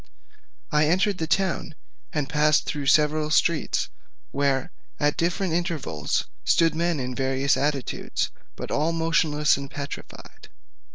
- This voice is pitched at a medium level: Yes, medium, 150 Hz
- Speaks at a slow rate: Yes, slow, 125 wpm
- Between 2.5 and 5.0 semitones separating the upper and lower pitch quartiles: Yes, average, 2.8 semitones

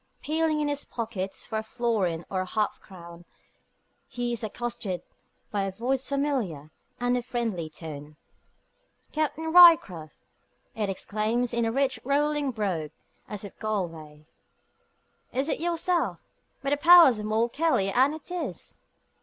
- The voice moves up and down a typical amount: No, wide, 6.6 semitones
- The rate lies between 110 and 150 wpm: Yes, average, 145 wpm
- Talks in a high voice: Yes, high, 235 Hz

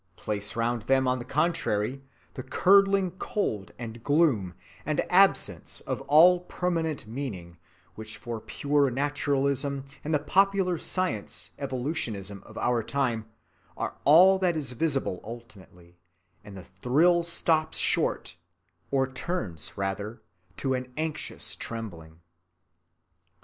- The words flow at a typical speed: No, slow, 120 wpm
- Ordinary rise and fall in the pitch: No, wide, 6.5 semitones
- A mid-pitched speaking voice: No, low, 130 Hz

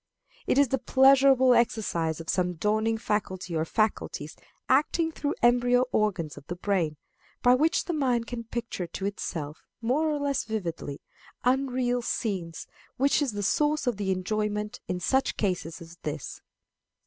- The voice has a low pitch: No, high, 220 Hz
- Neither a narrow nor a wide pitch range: No, wide, 6.2 semitones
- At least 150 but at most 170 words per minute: Yes, average, 155 wpm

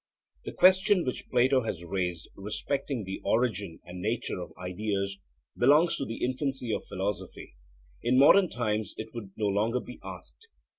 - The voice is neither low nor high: No, low, 110 Hz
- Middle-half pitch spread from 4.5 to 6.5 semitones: Yes, average, 4.9 semitones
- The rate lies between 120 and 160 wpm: Yes, average, 155 wpm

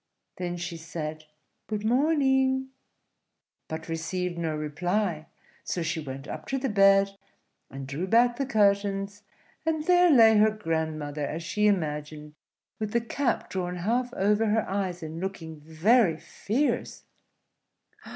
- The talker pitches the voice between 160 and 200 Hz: Yes, high, 190 Hz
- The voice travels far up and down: Yes, wide, 5.8 semitones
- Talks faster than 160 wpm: No, slow, 135 wpm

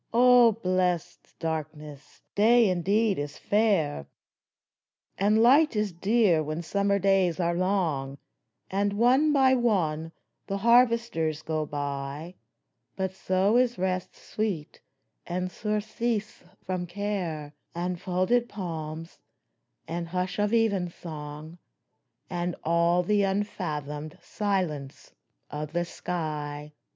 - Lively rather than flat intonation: No, average, 4.7 semitones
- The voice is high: No, medium, 180 Hz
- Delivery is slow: Yes, slow, 105 wpm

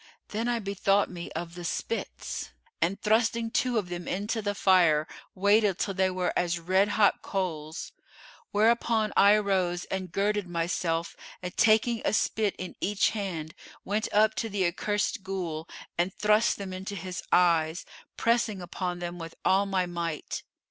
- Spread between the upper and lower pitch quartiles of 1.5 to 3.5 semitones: Yes, average, 3.1 semitones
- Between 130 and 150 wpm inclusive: No, average, 160 wpm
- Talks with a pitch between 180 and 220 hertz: Yes, high, 190 Hz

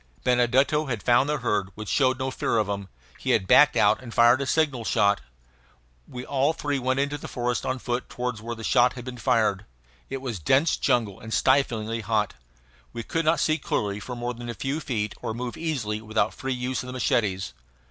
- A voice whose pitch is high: No, low, 120 Hz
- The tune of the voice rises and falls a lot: No, average, 3.3 semitones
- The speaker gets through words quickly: Yes, fast, 210 wpm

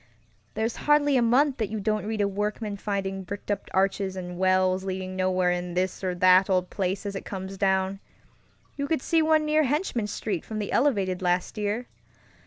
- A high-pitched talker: Yes, high, 195 Hz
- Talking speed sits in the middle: Yes, average, 190 wpm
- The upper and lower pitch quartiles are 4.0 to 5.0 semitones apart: No, average, 3.0 semitones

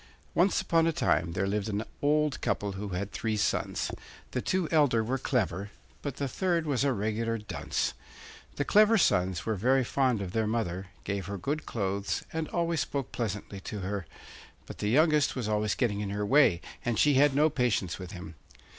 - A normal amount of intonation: No, wide, 6.2 semitones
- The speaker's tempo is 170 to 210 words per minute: Yes, average, 190 wpm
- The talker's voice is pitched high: No, low, 115 Hz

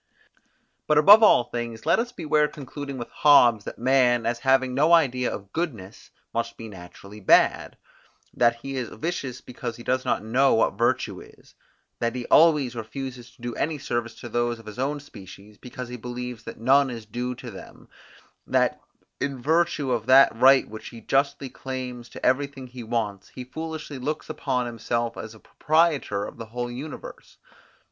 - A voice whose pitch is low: Yes, low, 125 Hz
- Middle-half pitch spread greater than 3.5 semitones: No, average, 3.0 semitones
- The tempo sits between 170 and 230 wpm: Yes, average, 175 wpm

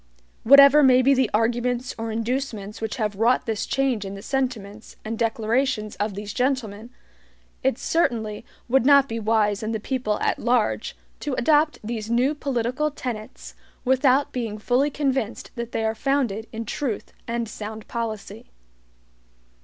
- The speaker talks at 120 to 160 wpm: Yes, average, 155 wpm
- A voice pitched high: Yes, high, 235 Hz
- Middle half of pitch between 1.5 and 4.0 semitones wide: Yes, average, 3.3 semitones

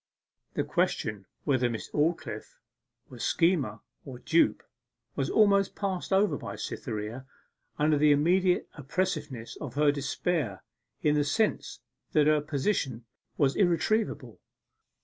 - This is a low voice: No, medium, 150 Hz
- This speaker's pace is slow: Yes, slow, 120 wpm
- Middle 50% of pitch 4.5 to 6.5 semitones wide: Yes, average, 5.3 semitones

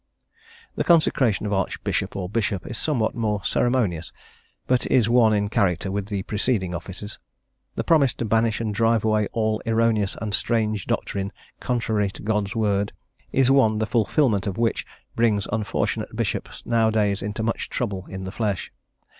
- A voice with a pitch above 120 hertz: No, low, 110 Hz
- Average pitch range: No, narrow, 2.3 semitones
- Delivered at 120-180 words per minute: Yes, average, 160 wpm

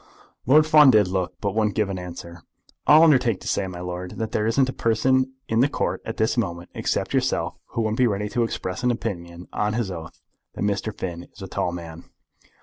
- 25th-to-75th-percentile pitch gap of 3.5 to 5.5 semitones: Yes, average, 4.7 semitones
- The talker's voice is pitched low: Yes, low, 105 Hz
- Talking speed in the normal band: No, fast, 220 wpm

